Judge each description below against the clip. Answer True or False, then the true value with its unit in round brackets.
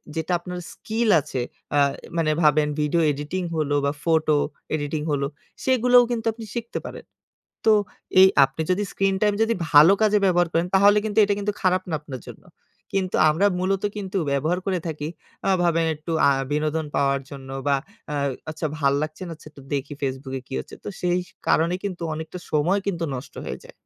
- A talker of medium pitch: True (165 Hz)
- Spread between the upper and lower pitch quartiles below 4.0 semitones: False (4.6 semitones)